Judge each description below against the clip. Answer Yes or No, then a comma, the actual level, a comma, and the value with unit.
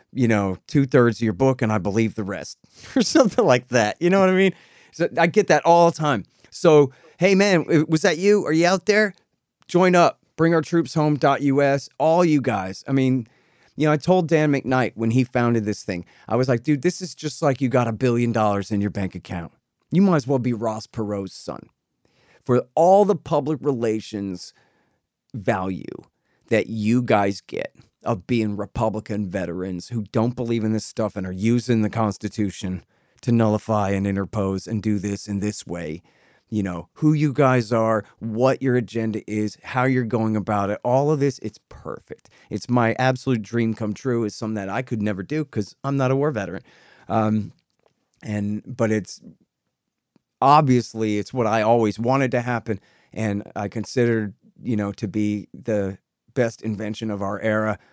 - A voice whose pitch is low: Yes, low, 115 Hz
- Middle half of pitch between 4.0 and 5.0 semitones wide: Yes, average, 4.7 semitones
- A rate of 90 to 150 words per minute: No, average, 195 wpm